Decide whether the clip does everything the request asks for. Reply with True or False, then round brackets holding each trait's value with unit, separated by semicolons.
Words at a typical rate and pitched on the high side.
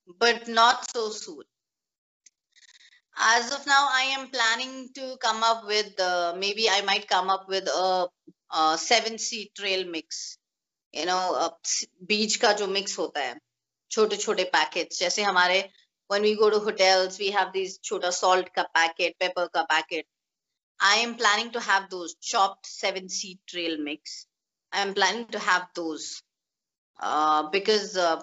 True (160 wpm; 195 Hz)